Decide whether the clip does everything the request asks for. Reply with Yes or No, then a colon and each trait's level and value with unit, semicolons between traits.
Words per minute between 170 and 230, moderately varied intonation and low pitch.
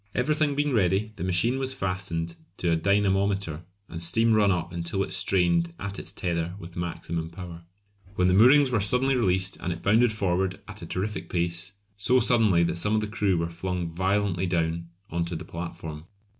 Yes: average, 190 wpm; average, 3.6 semitones; very low, 95 Hz